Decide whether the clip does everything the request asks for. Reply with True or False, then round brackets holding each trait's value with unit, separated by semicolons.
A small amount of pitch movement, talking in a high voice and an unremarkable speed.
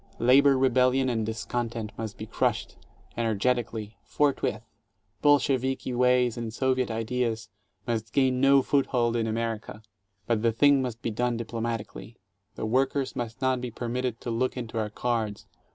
False (2.3 semitones; 120 Hz; 150 wpm)